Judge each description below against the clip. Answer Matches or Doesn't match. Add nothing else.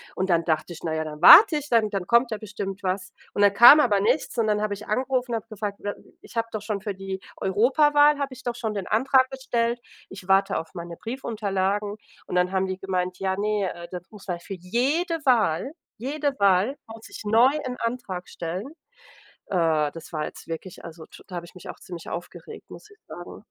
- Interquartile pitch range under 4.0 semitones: Doesn't match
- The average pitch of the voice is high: Matches